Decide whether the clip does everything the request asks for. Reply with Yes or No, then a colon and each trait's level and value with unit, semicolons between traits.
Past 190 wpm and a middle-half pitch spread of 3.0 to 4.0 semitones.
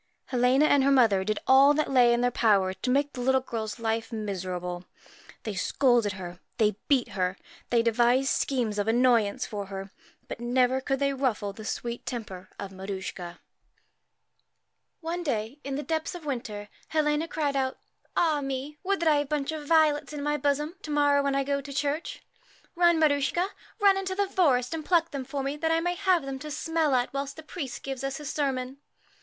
No: average, 200 wpm; average, 4.7 semitones